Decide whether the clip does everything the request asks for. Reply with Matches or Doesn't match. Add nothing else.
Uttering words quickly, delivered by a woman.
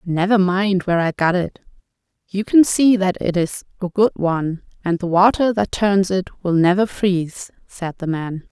Doesn't match